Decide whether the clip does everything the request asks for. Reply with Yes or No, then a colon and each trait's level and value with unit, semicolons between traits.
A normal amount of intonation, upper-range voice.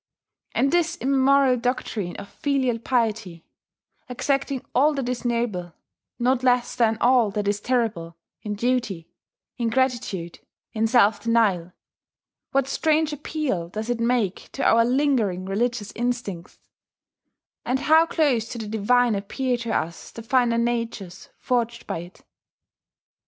Yes: average, 3.7 semitones; high, 235 Hz